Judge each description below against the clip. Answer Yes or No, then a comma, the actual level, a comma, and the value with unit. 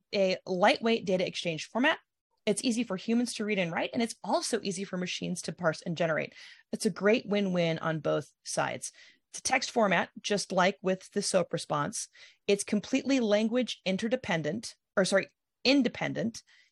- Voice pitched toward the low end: No, high, 205 Hz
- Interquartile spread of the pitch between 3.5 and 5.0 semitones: Yes, average, 4.0 semitones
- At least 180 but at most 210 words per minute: No, average, 170 wpm